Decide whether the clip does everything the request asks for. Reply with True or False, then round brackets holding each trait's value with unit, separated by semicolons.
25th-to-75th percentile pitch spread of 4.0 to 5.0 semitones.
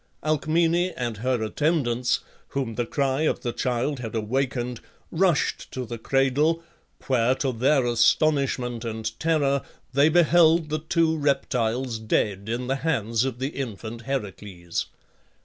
True (4.4 semitones)